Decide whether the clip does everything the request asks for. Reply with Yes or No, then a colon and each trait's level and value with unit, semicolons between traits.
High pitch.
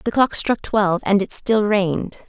Yes: high, 205 Hz